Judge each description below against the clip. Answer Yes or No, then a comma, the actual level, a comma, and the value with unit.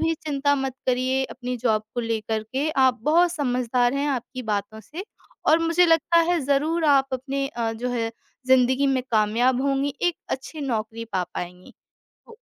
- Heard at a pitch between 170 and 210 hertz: No, very high, 260 Hz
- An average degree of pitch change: Yes, average, 3.4 semitones